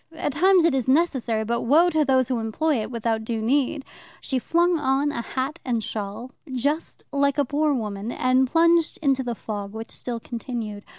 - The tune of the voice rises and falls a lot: No, average, 4.4 semitones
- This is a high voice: Yes, very high, 260 Hz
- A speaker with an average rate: Yes, average, 190 wpm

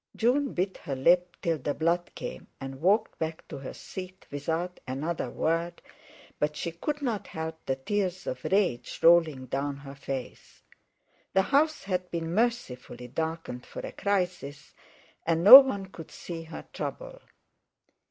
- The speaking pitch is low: No, medium, 170 Hz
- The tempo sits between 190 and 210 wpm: No, average, 150 wpm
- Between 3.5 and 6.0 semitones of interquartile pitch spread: Yes, average, 5.1 semitones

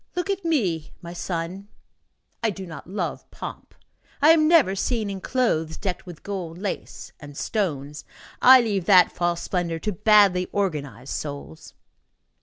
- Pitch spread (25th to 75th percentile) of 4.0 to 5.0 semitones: Yes, average, 4.4 semitones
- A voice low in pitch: No, medium, 185 Hz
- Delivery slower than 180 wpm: Yes, average, 150 wpm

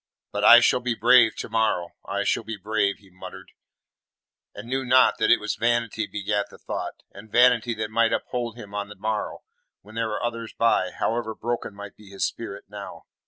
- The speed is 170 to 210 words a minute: Yes, average, 200 wpm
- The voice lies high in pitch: No, low, 110 Hz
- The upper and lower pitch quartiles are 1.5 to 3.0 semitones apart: Yes, narrow, 2.5 semitones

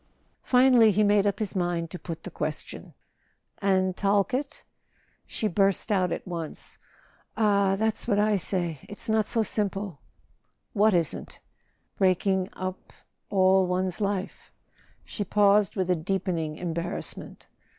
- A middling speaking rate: No, slow, 130 wpm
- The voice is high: Yes, high, 195 Hz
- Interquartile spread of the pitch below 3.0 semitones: Yes, narrow, 2.4 semitones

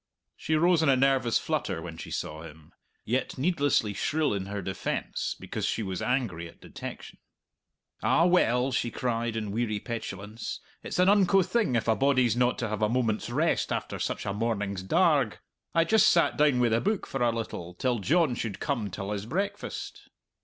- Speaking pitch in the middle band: No, low, 120 Hz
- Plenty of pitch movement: Yes, wide, 5.7 semitones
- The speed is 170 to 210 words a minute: Yes, average, 190 wpm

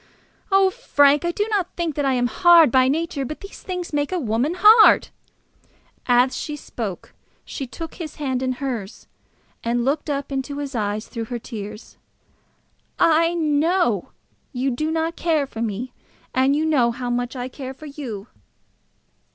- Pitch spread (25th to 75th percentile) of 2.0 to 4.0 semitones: No, average, 4.8 semitones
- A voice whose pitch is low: No, very high, 275 Hz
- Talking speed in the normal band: Yes, average, 170 wpm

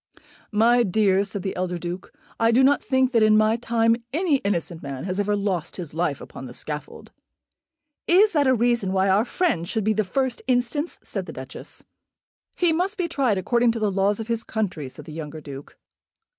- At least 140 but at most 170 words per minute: No, average, 200 wpm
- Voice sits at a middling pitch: No, high, 215 Hz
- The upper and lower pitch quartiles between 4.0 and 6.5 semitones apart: Yes, average, 5.1 semitones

